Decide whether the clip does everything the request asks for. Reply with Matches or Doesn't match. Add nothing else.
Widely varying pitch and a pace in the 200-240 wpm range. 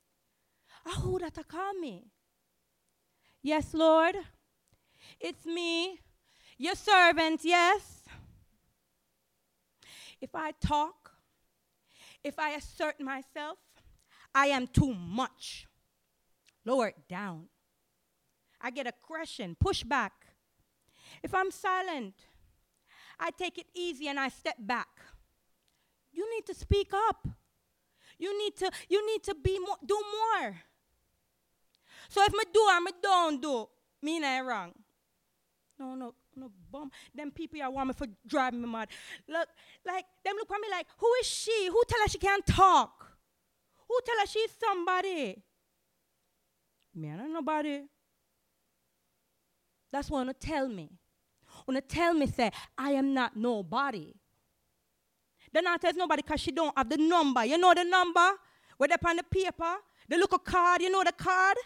Doesn't match